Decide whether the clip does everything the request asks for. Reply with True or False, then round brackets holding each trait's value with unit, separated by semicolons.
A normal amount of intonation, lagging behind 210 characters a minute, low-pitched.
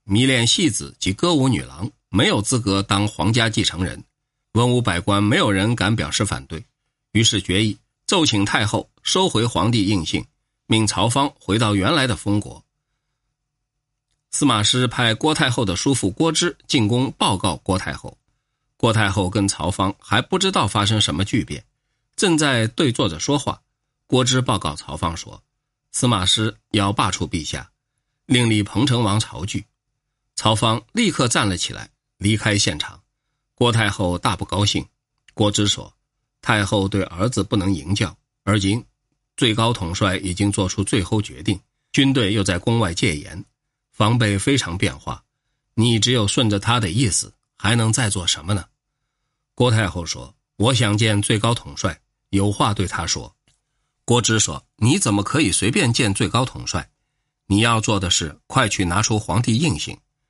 False (4.2 semitones; 235 characters per minute; 110 Hz)